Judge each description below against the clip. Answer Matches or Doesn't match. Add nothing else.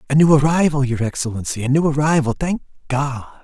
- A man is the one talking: Matches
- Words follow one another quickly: Doesn't match